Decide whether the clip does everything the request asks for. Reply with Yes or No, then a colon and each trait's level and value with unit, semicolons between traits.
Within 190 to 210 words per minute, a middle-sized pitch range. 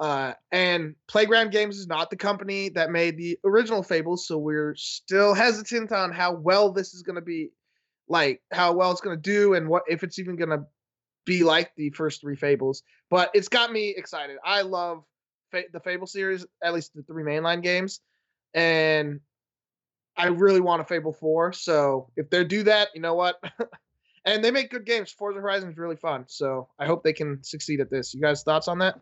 Yes: fast, 205 wpm; average, 4.1 semitones